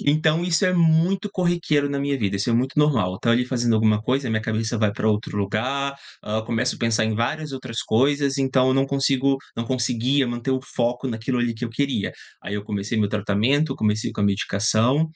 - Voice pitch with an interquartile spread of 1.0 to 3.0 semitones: No, average, 4.1 semitones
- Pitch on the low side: Yes, low, 125 Hz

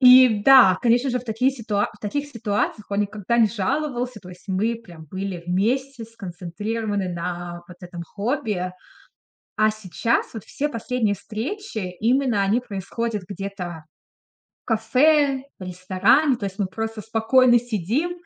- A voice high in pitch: Yes, high, 220 Hz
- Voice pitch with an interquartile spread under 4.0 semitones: No, average, 4.6 semitones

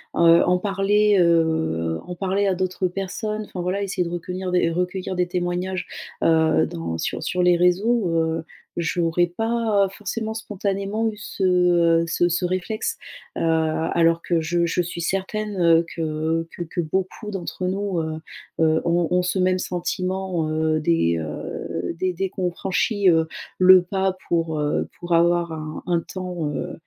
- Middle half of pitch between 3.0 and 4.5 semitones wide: No, narrow, 2.6 semitones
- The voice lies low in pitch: No, medium, 180 Hz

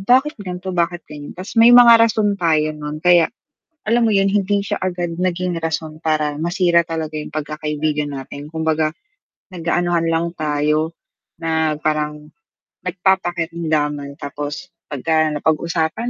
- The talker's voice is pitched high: No, medium, 165 Hz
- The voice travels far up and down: No, average, 3.1 semitones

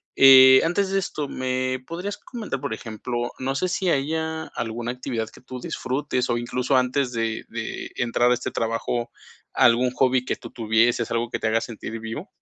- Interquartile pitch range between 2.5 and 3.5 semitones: Yes, average, 2.9 semitones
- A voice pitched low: Yes, low, 125 Hz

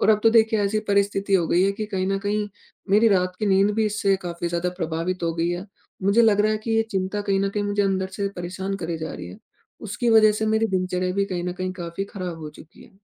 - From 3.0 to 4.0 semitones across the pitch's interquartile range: No, narrow, 2.5 semitones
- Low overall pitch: No, high, 195 Hz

